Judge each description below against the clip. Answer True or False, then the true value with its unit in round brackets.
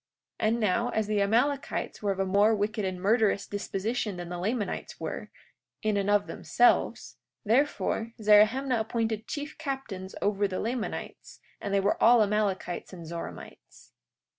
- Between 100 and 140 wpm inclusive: False (155 wpm)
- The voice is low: False (210 Hz)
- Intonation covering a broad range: False (2.8 semitones)